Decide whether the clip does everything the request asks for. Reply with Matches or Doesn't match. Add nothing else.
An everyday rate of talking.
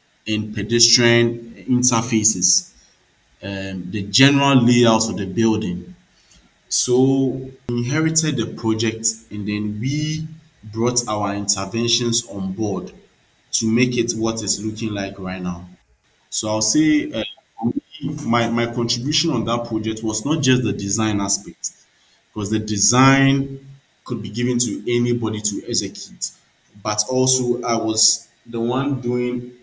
Doesn't match